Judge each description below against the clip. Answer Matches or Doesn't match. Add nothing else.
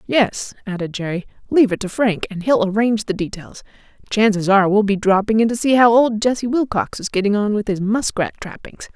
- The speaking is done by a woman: Matches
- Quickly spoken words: Matches